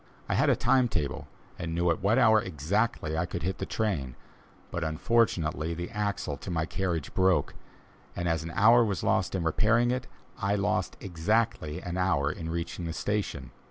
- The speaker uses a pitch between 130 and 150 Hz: No, very low, 90 Hz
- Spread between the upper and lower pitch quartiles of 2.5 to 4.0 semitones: No, average, 4.6 semitones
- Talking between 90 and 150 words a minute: No, average, 185 wpm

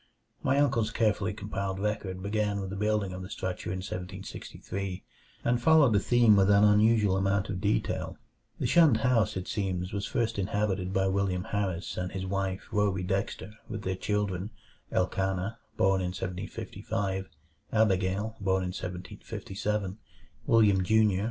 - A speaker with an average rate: Yes, average, 150 wpm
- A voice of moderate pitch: No, low, 100 Hz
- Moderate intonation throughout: No, narrow, 2.2 semitones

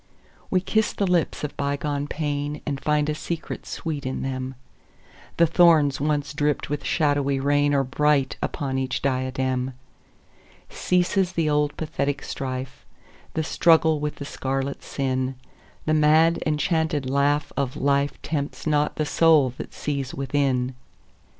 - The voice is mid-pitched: Yes, medium, 145 Hz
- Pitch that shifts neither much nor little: No, narrow, 2.2 semitones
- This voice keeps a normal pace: No, slow, 120 wpm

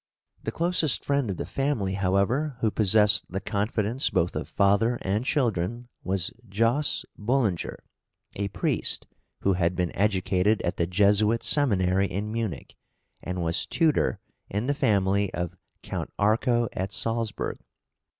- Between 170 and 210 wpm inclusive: No, average, 140 wpm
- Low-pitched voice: Yes, low, 105 Hz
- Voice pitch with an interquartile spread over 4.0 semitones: No, average, 3.7 semitones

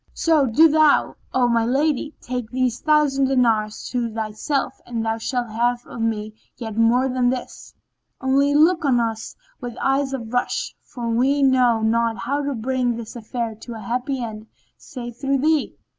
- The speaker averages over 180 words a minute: No, average, 175 wpm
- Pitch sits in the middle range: No, high, 245 Hz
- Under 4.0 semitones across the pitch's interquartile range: Yes, average, 3.0 semitones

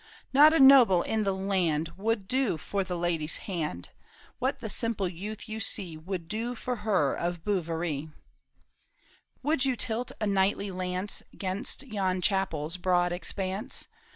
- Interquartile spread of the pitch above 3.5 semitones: Yes, average, 4.0 semitones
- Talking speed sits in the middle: Yes, average, 155 wpm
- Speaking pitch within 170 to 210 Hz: Yes, high, 190 Hz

